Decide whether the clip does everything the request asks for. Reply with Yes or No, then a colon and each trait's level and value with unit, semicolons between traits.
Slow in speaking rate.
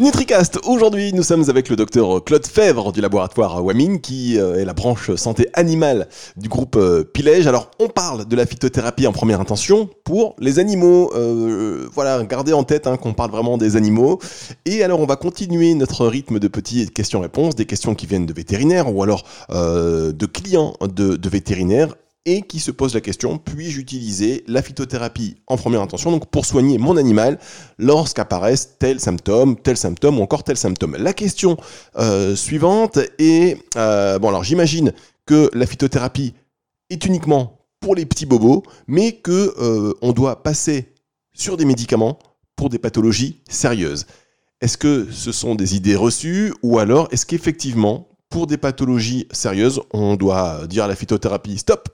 No: average, 170 wpm